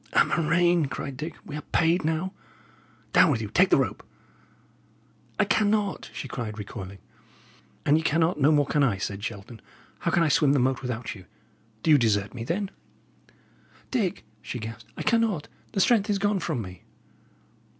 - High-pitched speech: No, medium, 150 Hz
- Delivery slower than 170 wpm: No, average, 175 wpm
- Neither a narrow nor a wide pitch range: No, wide, 7.3 semitones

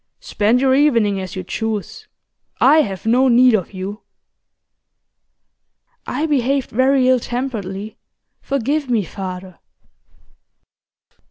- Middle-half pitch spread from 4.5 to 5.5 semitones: Yes, average, 4.9 semitones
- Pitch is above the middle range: Yes, high, 235 Hz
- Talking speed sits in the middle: No, slow, 105 wpm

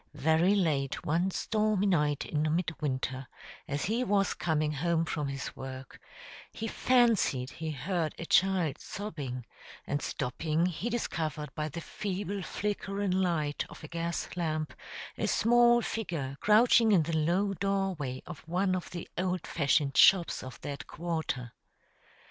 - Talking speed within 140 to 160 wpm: Yes, average, 145 wpm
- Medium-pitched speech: Yes, medium, 170 Hz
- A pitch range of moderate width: Yes, average, 4.6 semitones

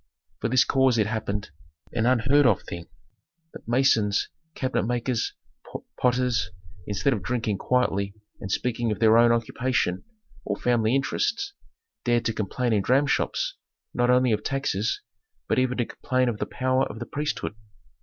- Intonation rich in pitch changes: No, average, 2.9 semitones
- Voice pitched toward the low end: Yes, low, 120 Hz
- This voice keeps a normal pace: Yes, average, 155 wpm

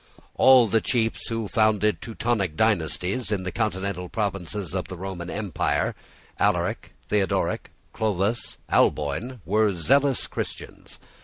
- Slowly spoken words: Yes, slow, 120 wpm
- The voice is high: No, low, 105 Hz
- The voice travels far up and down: No, average, 3.5 semitones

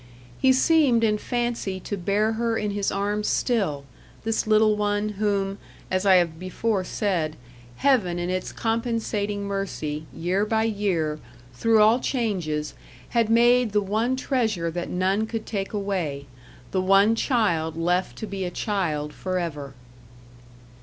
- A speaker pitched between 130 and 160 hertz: No, high, 200 Hz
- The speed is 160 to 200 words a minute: No, average, 145 wpm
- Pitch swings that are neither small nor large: Yes, average, 3.8 semitones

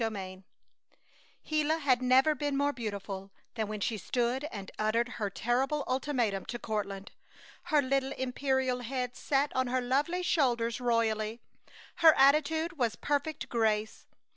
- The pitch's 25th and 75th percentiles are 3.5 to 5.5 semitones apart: Yes, average, 4.4 semitones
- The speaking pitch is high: Yes, very high, 250 Hz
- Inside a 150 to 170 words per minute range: No, average, 140 wpm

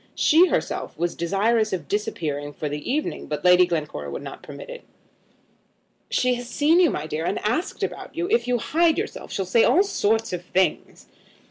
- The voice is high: Yes, high, 215 Hz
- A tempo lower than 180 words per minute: No, average, 190 wpm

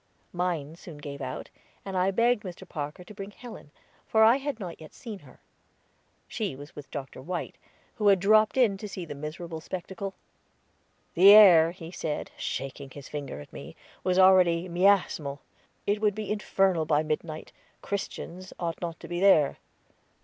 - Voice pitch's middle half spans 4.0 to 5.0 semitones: Yes, average, 4.4 semitones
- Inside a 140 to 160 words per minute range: No, average, 170 wpm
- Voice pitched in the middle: Yes, medium, 180 Hz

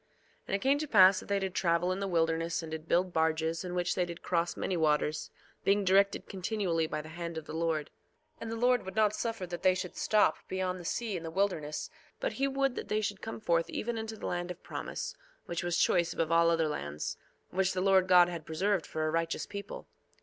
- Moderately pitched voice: Yes, medium, 180 Hz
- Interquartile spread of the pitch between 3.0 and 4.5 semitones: Yes, average, 3.3 semitones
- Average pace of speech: No, fast, 240 wpm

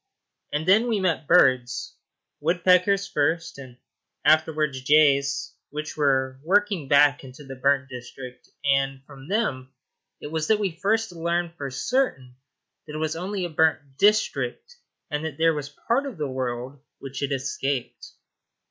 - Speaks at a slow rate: No, average, 150 wpm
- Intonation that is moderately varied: Yes, average, 4.6 semitones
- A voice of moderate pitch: Yes, medium, 150 Hz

